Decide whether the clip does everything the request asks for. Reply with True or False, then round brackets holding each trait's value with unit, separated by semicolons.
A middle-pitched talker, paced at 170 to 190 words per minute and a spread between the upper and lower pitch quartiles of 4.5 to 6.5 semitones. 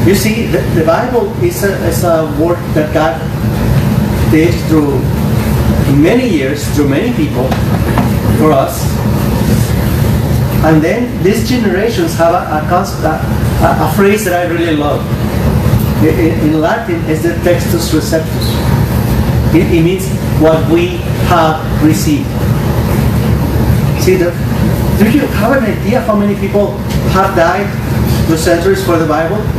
False (160 Hz; 135 wpm; 5.2 semitones)